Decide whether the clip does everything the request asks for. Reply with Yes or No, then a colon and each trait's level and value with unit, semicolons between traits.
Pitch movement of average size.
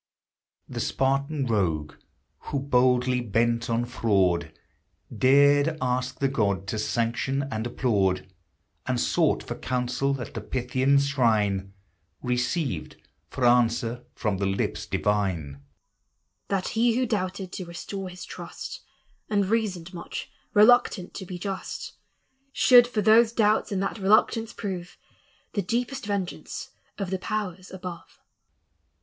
No: wide, 8.6 semitones